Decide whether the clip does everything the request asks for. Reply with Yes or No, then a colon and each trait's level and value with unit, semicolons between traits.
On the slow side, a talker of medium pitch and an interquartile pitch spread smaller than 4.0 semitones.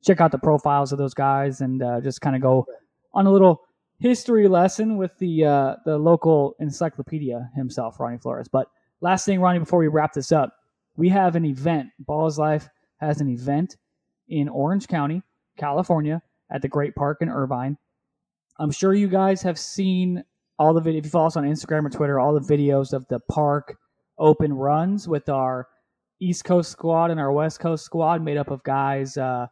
No: average, 195 wpm; medium, 150 Hz; average, 3.5 semitones